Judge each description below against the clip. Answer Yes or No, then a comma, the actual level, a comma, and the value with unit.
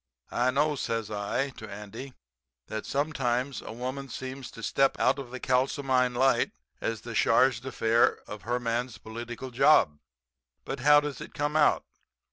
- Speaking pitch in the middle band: No, low, 125 Hz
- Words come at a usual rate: Yes, average, 160 wpm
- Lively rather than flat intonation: No, average, 3.0 semitones